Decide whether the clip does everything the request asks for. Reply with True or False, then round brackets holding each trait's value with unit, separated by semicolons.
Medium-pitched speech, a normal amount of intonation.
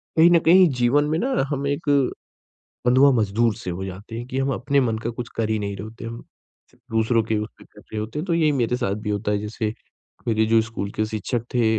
False (115 Hz; 3.7 semitones)